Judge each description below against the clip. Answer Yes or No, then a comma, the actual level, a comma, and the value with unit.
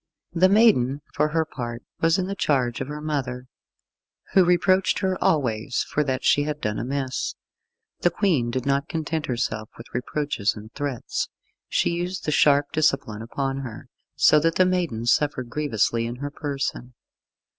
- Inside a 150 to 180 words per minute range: Yes, average, 165 wpm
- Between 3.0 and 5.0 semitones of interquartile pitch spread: Yes, average, 4.6 semitones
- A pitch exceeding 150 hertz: No, medium, 140 Hz